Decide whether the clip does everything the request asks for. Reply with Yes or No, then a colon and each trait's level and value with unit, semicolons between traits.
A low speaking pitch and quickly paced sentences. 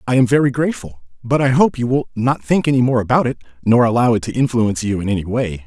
Yes: low, 120 Hz; fast, 255 wpm